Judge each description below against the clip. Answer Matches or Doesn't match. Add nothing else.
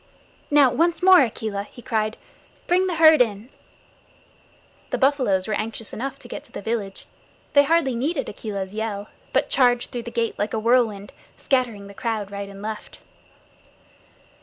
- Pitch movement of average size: Matches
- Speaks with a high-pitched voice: Matches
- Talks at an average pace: Matches